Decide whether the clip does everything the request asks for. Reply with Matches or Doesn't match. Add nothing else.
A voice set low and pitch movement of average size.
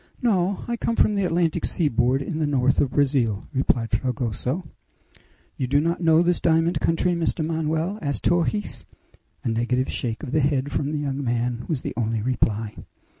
Doesn't match